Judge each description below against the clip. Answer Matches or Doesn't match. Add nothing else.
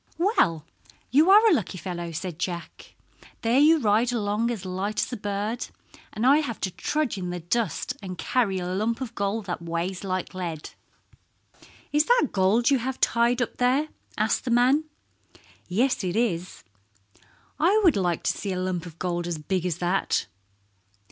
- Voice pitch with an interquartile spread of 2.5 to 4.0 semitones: Doesn't match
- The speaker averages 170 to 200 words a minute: Matches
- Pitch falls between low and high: Doesn't match